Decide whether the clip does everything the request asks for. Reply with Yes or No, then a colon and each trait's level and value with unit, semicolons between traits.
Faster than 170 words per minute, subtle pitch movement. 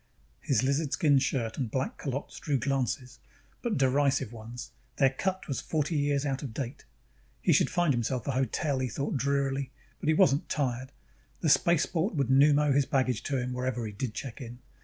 Yes: average, 180 wpm; narrow, 2.2 semitones